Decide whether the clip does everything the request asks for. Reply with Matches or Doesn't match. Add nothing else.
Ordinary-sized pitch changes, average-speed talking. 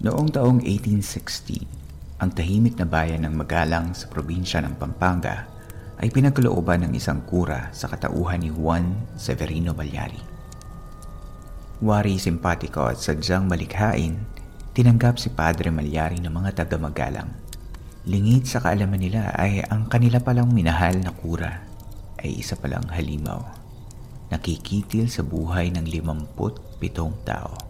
Matches